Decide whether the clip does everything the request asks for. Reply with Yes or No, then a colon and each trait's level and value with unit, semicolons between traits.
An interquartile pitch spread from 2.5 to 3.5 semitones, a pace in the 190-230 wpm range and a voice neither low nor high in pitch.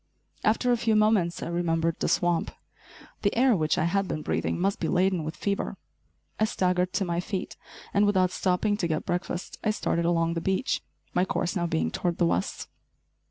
Yes: average, 3.0 semitones; average, 195 wpm; medium, 180 Hz